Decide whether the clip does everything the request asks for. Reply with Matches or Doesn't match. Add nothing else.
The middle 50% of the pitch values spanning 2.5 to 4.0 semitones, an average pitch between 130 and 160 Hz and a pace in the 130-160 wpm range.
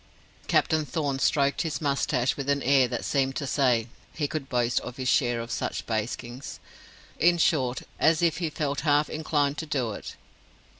Doesn't match